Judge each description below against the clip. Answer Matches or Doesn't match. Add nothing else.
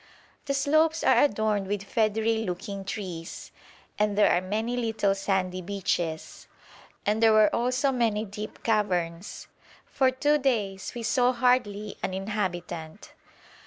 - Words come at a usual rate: Doesn't match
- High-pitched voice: Matches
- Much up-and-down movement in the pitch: Doesn't match